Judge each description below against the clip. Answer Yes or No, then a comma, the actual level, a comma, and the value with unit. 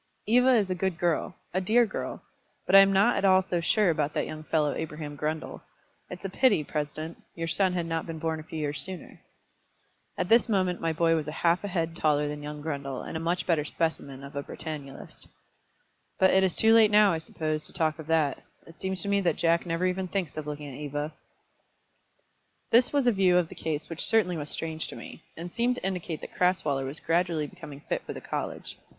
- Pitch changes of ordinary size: Yes, average, 3.6 semitones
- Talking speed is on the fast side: Yes, fast, 225 wpm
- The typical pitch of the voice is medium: Yes, medium, 165 Hz